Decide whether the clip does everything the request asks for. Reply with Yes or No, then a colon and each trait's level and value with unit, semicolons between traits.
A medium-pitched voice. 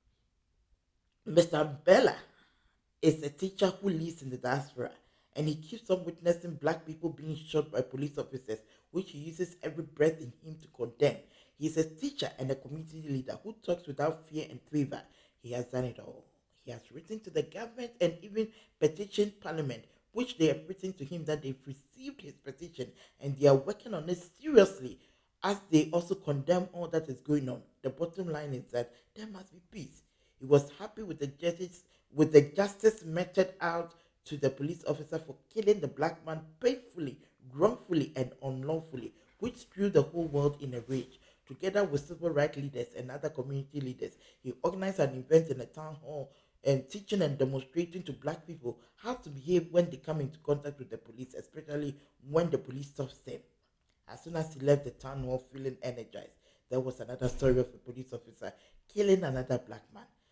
Yes: medium, 150 Hz